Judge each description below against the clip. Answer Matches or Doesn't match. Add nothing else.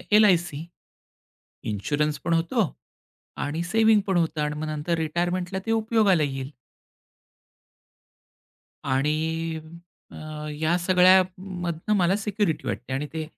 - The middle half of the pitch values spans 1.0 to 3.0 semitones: Doesn't match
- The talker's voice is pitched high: Doesn't match